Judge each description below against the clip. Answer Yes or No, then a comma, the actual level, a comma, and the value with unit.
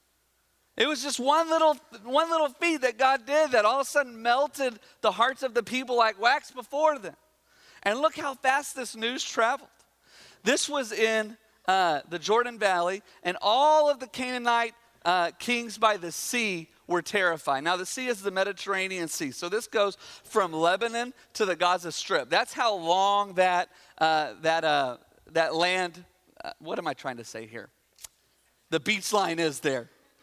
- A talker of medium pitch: No, high, 220 Hz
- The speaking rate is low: No, average, 180 wpm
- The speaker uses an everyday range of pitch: No, wide, 6.7 semitones